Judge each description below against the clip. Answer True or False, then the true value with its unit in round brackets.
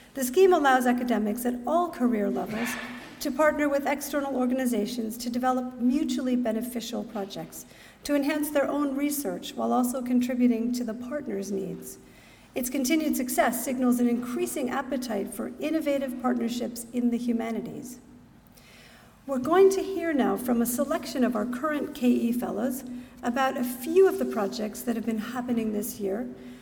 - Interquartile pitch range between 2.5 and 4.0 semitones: True (3.2 semitones)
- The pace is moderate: True (155 wpm)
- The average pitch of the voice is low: False (250 Hz)